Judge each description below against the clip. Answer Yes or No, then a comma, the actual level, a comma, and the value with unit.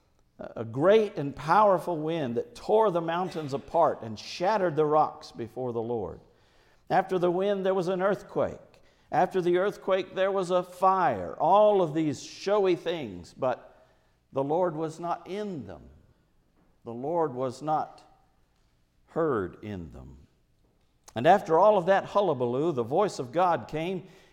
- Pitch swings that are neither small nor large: No, wide, 7.9 semitones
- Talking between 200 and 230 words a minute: No, average, 150 wpm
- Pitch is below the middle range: No, medium, 165 Hz